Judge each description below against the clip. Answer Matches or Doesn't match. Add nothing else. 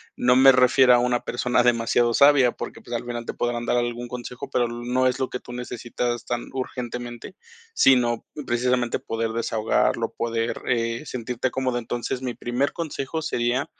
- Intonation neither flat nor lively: Doesn't match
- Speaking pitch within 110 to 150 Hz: Matches